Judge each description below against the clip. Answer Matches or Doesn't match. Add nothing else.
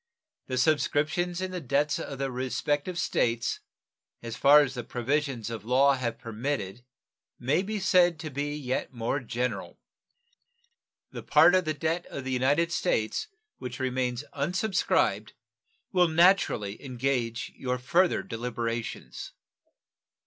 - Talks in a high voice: Doesn't match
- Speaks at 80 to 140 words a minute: Matches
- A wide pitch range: Doesn't match